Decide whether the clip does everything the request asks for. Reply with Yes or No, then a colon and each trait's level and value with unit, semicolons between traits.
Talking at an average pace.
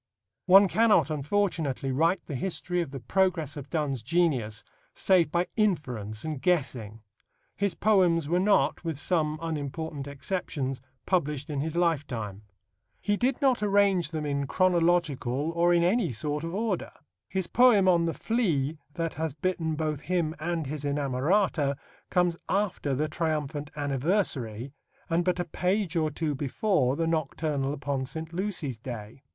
Yes: average, 150 wpm